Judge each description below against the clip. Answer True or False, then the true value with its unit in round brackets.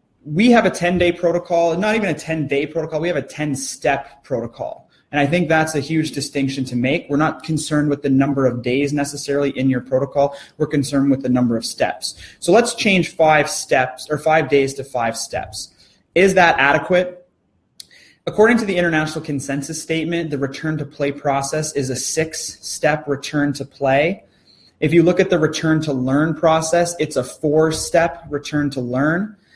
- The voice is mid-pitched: True (150 Hz)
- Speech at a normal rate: True (190 wpm)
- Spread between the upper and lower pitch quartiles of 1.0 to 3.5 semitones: True (3.0 semitones)